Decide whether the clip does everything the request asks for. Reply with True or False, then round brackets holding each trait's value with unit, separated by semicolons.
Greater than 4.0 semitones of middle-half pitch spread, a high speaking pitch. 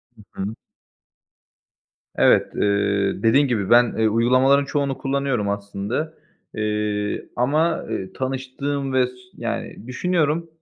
False (4.9 semitones; 125 Hz)